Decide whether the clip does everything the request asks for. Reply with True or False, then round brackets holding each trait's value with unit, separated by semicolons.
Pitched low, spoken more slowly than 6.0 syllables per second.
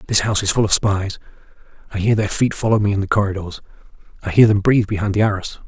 False (100 Hz; 7.1 syllables/s)